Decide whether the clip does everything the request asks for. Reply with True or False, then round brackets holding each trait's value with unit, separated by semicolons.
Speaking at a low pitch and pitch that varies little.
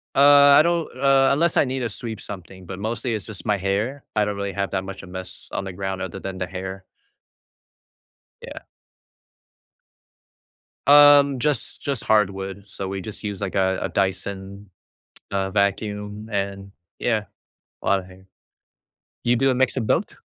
False (100 Hz; 3.7 semitones)